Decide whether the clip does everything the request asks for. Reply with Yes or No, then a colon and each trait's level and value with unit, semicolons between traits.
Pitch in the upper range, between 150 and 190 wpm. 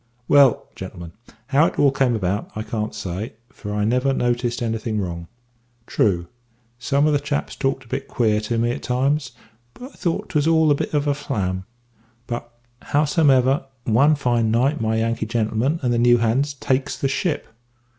No: low, 120 Hz; average, 180 wpm